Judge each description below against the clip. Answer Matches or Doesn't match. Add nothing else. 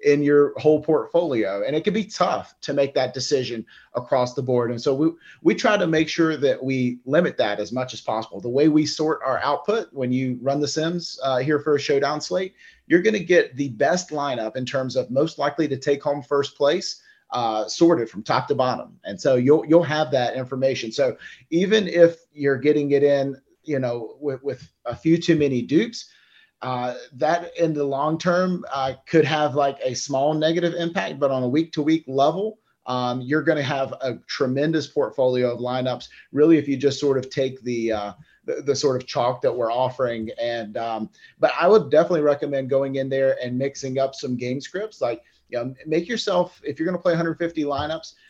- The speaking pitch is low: Doesn't match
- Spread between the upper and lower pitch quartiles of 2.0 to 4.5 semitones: Matches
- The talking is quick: Matches